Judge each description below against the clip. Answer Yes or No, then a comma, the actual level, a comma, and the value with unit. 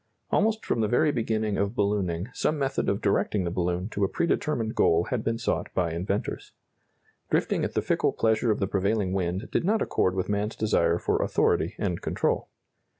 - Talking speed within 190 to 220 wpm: Yes, average, 195 wpm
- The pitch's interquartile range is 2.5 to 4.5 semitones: Yes, average, 3.7 semitones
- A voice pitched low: Yes, low, 105 Hz